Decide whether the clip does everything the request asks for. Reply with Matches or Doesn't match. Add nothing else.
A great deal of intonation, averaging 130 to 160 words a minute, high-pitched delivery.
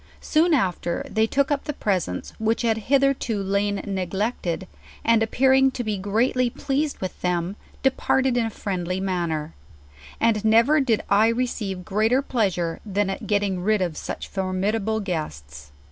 Doesn't match